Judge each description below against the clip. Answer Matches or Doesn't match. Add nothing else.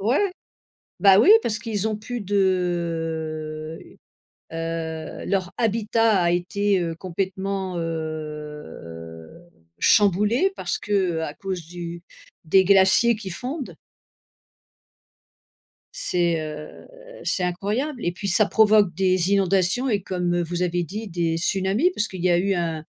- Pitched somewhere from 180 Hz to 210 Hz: Matches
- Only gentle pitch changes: Doesn't match